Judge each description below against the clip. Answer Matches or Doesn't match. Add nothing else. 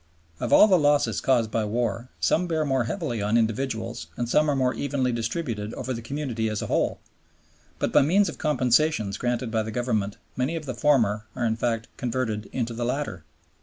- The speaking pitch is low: Matches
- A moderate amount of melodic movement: Matches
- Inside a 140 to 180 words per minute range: Doesn't match